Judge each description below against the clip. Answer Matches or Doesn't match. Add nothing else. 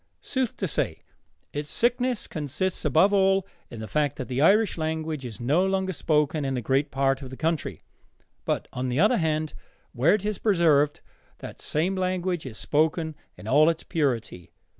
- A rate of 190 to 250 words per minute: Doesn't match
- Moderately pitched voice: Matches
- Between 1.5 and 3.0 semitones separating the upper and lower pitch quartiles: Doesn't match